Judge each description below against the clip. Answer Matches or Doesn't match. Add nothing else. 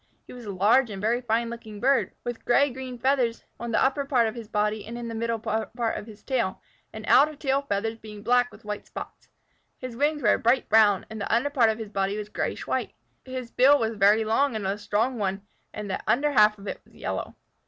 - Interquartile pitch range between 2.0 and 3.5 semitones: Matches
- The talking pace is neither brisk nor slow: Doesn't match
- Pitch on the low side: Doesn't match